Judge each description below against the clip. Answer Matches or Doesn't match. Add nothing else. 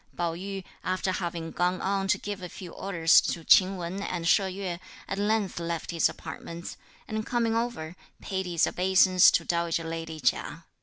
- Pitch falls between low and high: Matches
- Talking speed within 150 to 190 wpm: Matches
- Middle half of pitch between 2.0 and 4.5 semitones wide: Matches